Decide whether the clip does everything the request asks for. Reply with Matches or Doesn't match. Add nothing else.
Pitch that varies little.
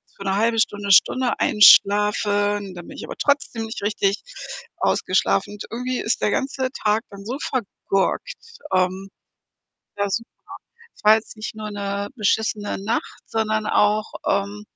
Matches